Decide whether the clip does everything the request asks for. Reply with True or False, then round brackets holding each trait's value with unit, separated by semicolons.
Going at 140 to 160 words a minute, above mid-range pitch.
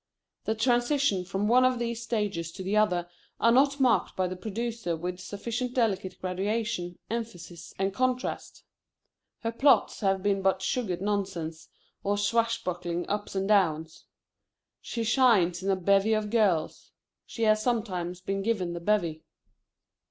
True (145 wpm; 205 Hz)